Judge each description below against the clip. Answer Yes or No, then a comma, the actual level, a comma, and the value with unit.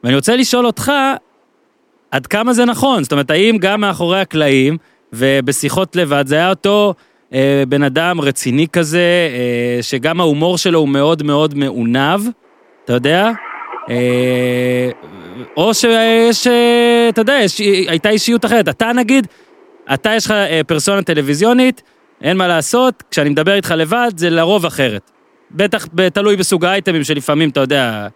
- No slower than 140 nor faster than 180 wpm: Yes, average, 145 wpm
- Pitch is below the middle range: No, medium, 175 Hz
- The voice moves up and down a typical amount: No, wide, 7.4 semitones